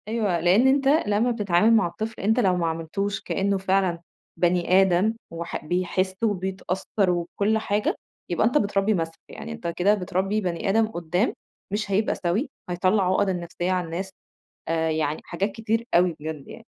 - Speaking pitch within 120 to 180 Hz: No, high, 190 Hz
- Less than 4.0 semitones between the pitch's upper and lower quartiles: Yes, average, 3.4 semitones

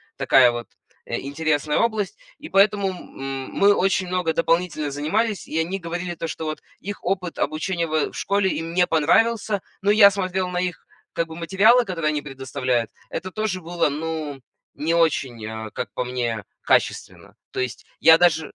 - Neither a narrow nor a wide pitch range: Yes, average, 4.4 semitones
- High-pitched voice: No, medium, 165 Hz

